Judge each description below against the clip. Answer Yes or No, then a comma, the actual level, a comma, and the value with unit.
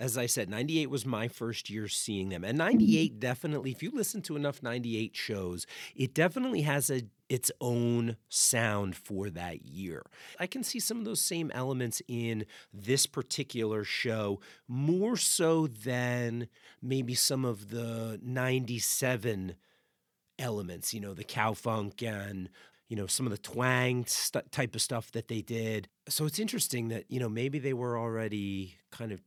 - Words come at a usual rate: Yes, average, 170 wpm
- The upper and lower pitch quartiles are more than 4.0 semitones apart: No, average, 3.7 semitones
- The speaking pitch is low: Yes, low, 120 Hz